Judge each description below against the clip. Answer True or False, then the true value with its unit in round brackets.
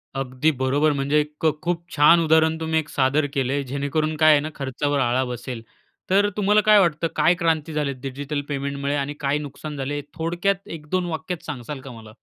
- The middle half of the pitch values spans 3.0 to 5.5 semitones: False (2.5 semitones)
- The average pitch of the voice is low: False (150 Hz)